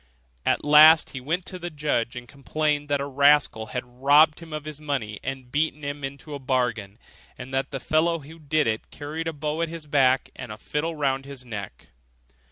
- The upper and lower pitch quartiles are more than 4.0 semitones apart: No, average, 3.0 semitones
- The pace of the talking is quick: Yes, fast, 210 wpm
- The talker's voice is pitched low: No, medium, 145 Hz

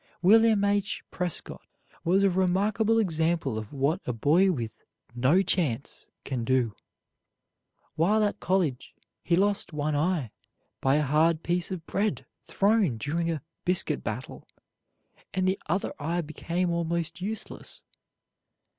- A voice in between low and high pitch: Yes, medium, 170 Hz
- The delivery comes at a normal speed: No, slow, 130 wpm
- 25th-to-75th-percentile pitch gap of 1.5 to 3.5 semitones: No, average, 4.6 semitones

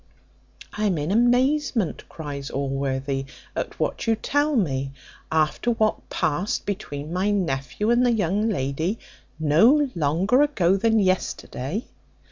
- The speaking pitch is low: No, high, 190 Hz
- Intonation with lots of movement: Yes, wide, 7.6 semitones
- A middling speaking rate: No, slow, 125 wpm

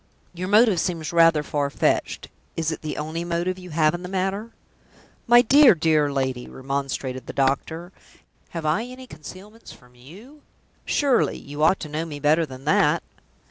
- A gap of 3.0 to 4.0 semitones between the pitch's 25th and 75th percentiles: No, average, 4.5 semitones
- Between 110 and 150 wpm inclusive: No, average, 170 wpm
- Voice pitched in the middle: Yes, medium, 165 Hz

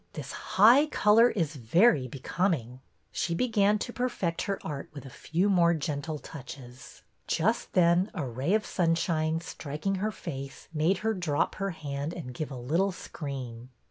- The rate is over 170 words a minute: No, average, 160 wpm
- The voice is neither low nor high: Yes, medium, 165 Hz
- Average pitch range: No, wide, 5.8 semitones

